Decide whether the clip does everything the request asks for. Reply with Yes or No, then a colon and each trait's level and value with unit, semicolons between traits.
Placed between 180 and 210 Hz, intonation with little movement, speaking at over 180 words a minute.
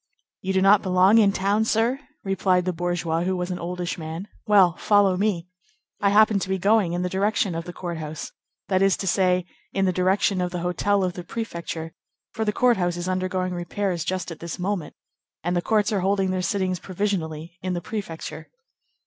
Yes: medium, 185 Hz; narrow, 2.2 semitones; fast, 205 wpm